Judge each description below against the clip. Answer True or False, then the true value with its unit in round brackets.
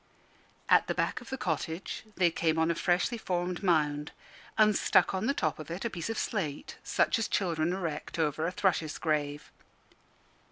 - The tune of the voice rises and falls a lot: False (3.4 semitones)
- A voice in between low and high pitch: True (170 Hz)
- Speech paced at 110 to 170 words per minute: False (185 wpm)